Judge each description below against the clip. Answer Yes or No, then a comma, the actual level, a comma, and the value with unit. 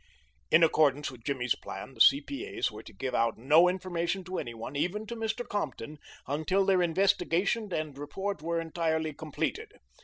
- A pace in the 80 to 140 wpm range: No, average, 165 wpm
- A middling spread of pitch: Yes, average, 4.9 semitones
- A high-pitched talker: No, medium, 165 Hz